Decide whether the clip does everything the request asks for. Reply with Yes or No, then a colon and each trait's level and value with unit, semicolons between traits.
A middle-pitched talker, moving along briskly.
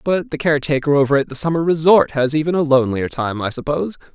Yes: medium, 150 Hz; fast, 215 wpm